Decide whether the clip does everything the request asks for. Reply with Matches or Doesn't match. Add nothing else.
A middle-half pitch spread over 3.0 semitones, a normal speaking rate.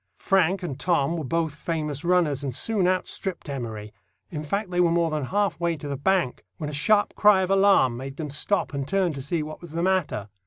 Doesn't match